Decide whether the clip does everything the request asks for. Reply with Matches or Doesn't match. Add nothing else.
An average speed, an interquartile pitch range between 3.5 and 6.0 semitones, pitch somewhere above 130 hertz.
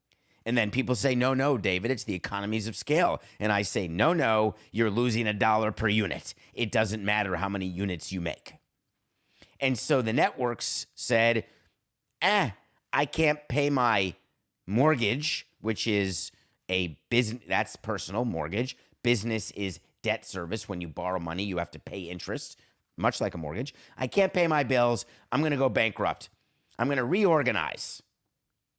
Doesn't match